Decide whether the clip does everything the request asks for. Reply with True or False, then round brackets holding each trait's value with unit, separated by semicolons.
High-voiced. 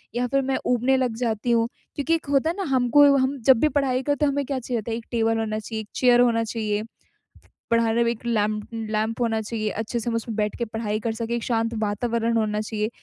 True (230 Hz)